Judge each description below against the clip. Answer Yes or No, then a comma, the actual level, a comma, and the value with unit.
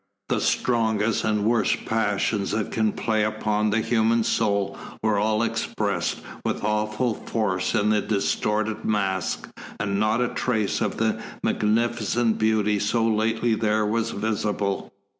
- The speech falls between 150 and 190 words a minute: No, average, 140 wpm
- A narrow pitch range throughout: Yes, narrow, 1.3 semitones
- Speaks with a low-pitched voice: Yes, low, 110 Hz